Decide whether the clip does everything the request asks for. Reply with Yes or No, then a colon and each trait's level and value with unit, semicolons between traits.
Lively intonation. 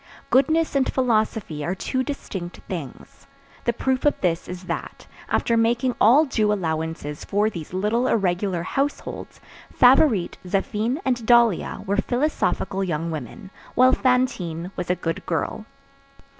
Yes: wide, 6.2 semitones